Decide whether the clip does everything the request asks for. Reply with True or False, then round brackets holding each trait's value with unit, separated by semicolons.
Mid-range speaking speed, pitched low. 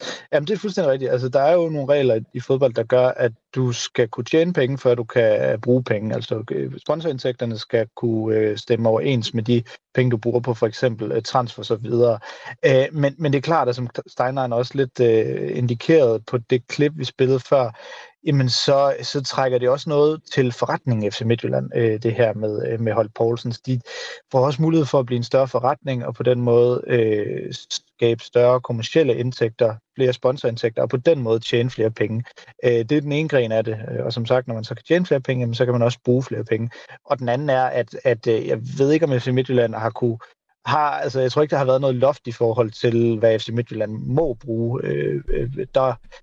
True (215 wpm; 125 Hz)